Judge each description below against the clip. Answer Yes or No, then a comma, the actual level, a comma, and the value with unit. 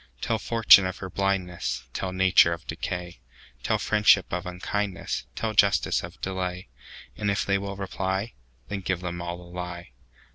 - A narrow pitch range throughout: Yes, narrow, 2.2 semitones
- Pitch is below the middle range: Yes, very low, 95 Hz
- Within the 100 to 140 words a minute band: Yes, slow, 135 wpm